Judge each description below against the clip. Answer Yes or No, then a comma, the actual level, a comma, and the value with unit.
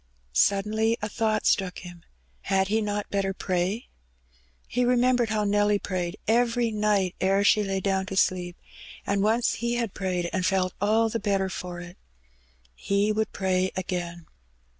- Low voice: No, high, 200 Hz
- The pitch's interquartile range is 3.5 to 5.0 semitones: No, average, 2.7 semitones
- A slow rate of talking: No, average, 160 wpm